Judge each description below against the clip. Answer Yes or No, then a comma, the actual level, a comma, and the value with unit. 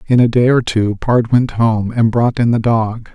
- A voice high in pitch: No, low, 115 Hz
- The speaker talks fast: Yes, fast, 250 wpm